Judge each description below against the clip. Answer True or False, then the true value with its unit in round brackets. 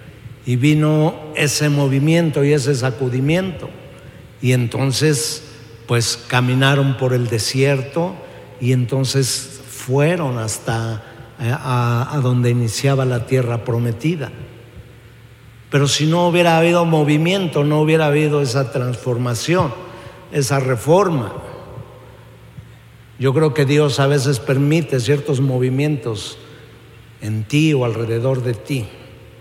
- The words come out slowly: True (110 wpm)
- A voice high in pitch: False (135 Hz)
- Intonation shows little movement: False (3.5 semitones)